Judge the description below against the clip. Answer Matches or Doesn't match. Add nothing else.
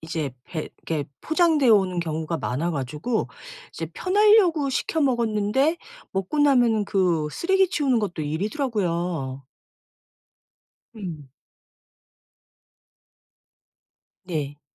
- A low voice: Doesn't match